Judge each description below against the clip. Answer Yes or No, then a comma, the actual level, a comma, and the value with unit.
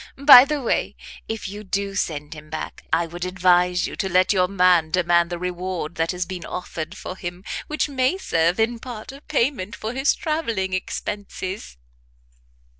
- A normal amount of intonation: Yes, average, 4.3 semitones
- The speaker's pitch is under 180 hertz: No, medium, 185 Hz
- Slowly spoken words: No, average, 175 wpm